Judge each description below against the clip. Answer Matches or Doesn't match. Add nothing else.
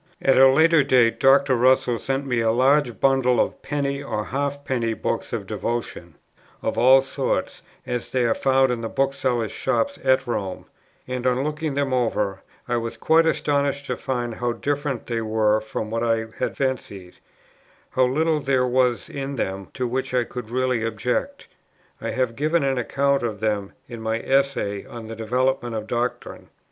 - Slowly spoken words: Doesn't match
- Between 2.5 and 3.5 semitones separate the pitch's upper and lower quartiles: Matches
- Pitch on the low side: Matches